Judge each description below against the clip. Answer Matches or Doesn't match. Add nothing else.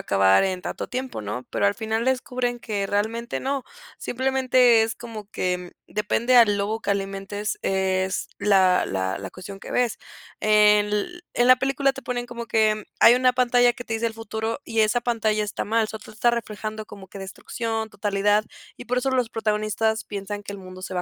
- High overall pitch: Matches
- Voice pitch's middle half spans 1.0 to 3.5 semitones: Matches